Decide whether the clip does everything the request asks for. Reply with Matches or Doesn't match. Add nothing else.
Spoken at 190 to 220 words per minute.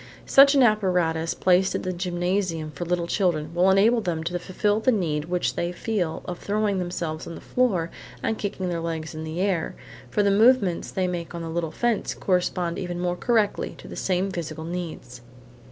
Matches